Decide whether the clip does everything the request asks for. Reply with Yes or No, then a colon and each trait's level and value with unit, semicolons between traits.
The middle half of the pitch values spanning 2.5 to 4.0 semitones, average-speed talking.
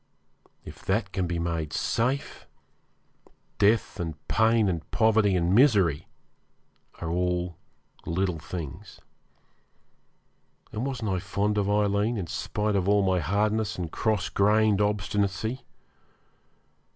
No: average, 3.2 semitones; slow, 115 wpm